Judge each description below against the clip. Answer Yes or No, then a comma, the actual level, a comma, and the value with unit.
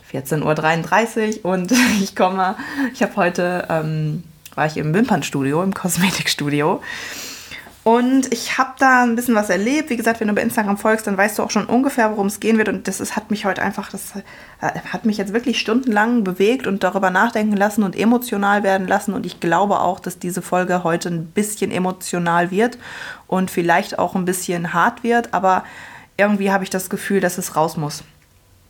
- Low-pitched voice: No, high, 195 Hz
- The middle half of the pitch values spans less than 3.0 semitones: No, average, 3.6 semitones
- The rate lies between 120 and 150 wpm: No, fast, 190 wpm